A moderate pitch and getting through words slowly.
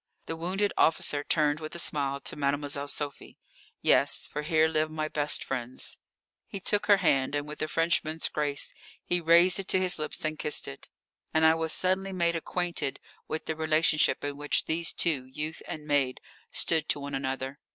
No: medium, 155 Hz; average, 185 wpm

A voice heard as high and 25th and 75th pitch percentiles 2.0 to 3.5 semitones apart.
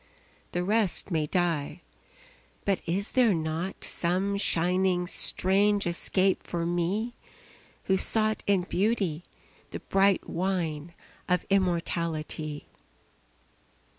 No: medium, 180 Hz; average, 2.7 semitones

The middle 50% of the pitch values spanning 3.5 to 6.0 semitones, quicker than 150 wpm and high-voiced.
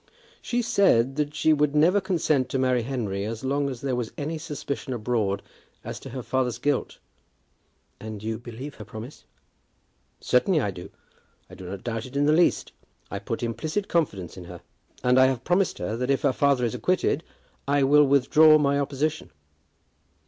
No: average, 4.6 semitones; average, 180 wpm; low, 135 Hz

